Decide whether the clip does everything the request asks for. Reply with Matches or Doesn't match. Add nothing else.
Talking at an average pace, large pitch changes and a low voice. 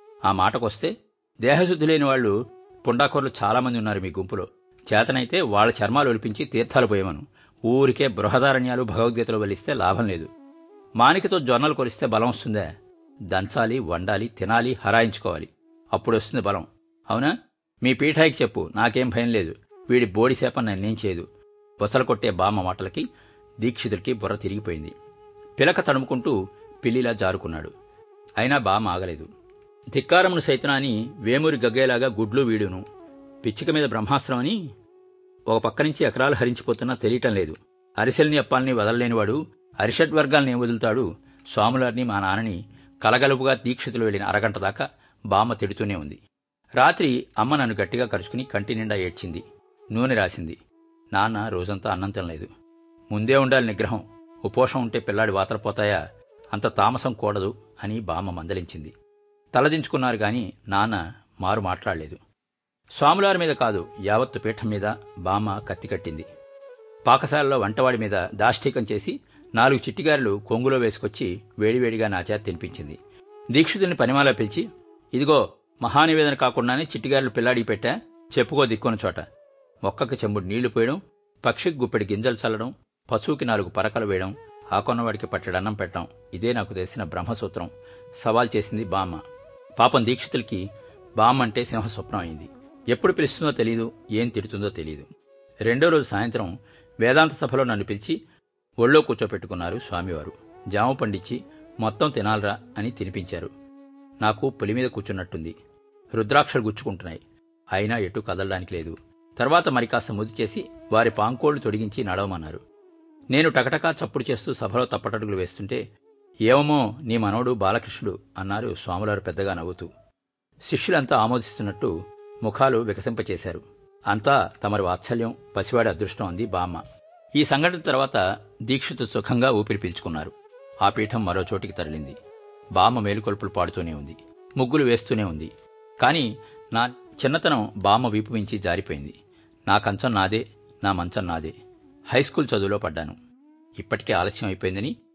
Matches